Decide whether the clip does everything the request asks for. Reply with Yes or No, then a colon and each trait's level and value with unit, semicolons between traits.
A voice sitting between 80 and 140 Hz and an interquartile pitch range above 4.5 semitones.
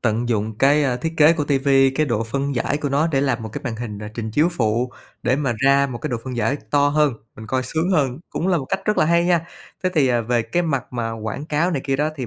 No: low, 135 Hz; average, 4.1 semitones